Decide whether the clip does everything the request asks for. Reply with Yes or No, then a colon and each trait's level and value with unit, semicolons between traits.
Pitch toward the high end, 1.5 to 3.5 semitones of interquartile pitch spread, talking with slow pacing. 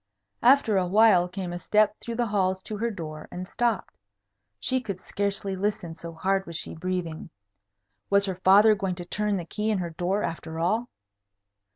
No: high, 195 Hz; average, 3.1 semitones; average, 185 wpm